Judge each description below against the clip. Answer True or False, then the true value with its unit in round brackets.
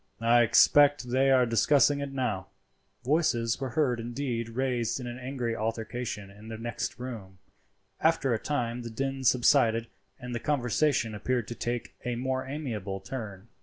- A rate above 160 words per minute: False (155 wpm)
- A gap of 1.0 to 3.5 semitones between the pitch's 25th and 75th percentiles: True (2.7 semitones)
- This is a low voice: True (120 Hz)